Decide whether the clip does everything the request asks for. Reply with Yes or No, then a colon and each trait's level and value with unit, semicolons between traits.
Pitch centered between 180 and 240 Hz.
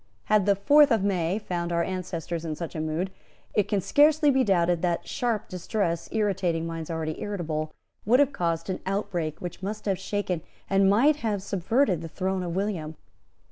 Yes: medium, 185 Hz